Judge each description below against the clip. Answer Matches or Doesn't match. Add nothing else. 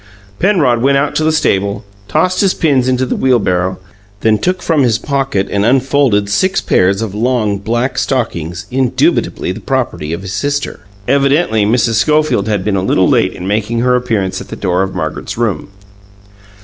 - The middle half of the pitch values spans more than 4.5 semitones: Matches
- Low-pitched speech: Matches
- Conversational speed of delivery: Matches